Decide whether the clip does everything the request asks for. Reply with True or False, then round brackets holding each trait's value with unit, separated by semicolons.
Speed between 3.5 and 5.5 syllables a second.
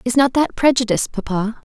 False (6.1 syllables/s)